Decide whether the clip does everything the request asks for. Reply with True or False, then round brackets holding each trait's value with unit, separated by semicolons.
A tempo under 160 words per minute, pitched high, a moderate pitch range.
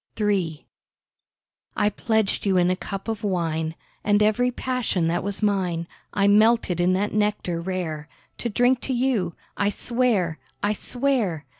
True (145 wpm; 200 Hz; 4.0 semitones)